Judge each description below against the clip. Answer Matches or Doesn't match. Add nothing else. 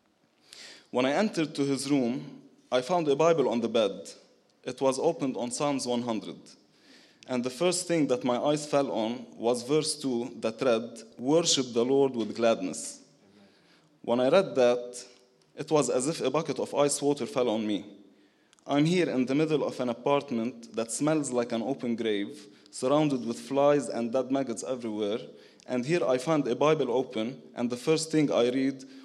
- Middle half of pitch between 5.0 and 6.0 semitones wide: Doesn't match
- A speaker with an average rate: Matches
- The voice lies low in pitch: Matches